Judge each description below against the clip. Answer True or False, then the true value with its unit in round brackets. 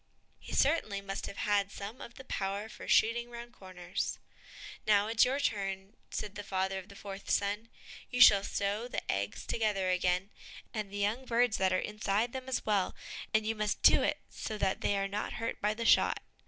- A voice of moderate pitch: False (205 Hz)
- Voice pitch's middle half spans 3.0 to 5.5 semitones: False (2.6 semitones)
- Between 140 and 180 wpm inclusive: False (200 wpm)